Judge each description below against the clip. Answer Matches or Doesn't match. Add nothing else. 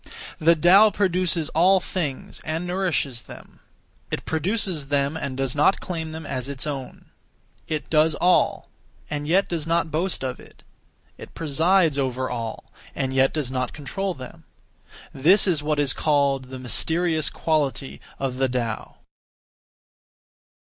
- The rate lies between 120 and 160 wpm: Matches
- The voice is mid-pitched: Matches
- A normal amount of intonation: Matches